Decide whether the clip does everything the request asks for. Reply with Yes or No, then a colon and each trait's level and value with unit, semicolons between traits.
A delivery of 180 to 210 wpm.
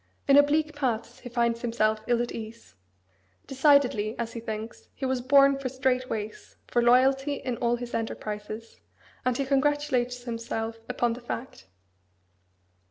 No: average, 150 wpm